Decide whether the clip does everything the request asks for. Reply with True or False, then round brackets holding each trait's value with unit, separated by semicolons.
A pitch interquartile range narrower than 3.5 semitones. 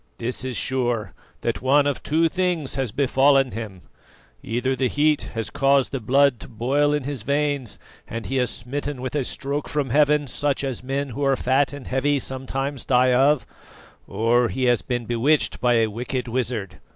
True (2.7 semitones)